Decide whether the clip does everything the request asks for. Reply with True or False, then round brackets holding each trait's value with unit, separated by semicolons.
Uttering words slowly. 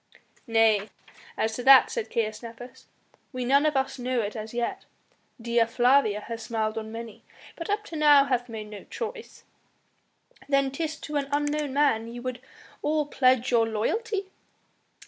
False (165 wpm)